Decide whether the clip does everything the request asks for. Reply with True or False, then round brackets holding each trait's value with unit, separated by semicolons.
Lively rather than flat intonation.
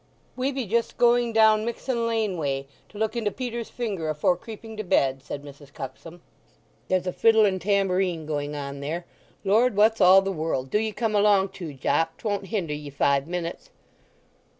True (5.9 semitones)